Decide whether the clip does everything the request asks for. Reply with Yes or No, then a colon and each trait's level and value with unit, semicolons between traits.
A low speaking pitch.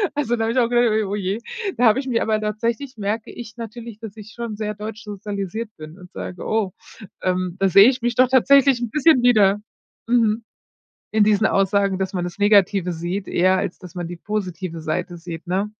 No: high, 210 Hz